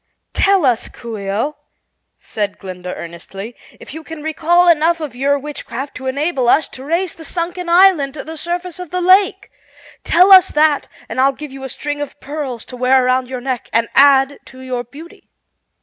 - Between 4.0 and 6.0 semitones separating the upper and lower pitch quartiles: Yes, average, 4.8 semitones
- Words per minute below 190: No, average, 195 wpm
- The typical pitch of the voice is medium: No, very high, 285 Hz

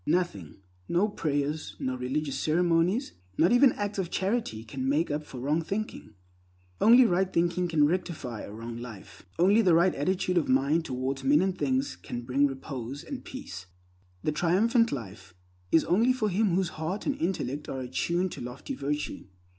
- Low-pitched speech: No, medium, 160 Hz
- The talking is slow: No, average, 170 wpm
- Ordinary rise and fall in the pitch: No, wide, 6.1 semitones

